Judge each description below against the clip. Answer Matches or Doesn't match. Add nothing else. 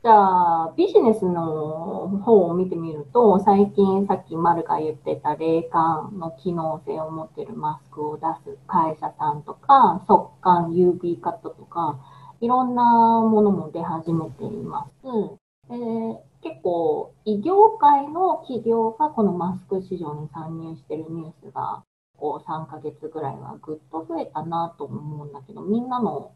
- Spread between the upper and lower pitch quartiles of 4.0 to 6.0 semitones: Matches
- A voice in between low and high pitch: Matches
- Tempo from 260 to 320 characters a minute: Matches